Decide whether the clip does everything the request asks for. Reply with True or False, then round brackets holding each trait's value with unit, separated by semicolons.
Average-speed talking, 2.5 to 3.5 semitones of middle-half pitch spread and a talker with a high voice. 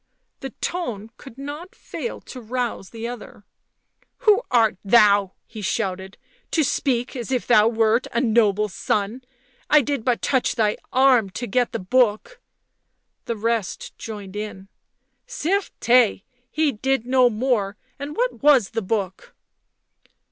False (155 wpm; 4.2 semitones; 235 Hz)